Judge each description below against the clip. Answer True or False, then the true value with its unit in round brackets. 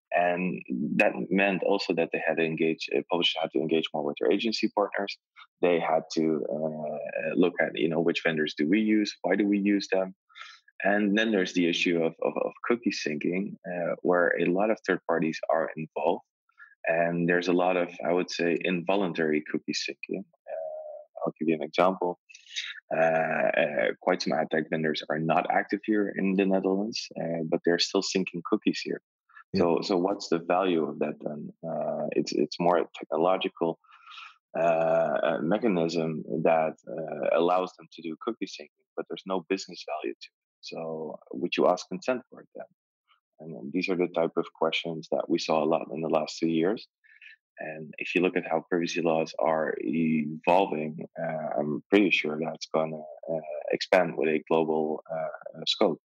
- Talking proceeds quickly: False (185 wpm)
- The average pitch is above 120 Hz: False (85 Hz)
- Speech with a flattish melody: False (3.1 semitones)